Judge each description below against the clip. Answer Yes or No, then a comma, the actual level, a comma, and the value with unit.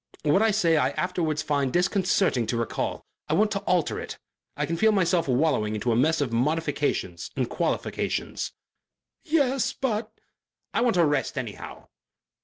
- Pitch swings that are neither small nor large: No, wide, 7.2 semitones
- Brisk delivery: No, average, 165 wpm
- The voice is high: No, medium, 165 Hz